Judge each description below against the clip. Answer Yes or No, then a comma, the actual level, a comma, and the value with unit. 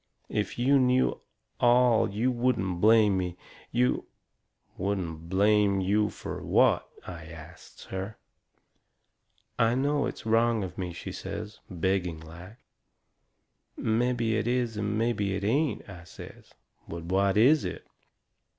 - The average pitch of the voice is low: Yes, low, 105 Hz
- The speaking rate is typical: No, slow, 130 wpm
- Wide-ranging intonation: No, average, 4.2 semitones